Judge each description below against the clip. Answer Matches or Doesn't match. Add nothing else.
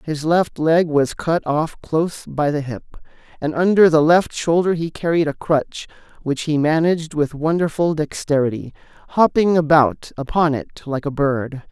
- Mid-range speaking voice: Matches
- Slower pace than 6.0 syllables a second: Matches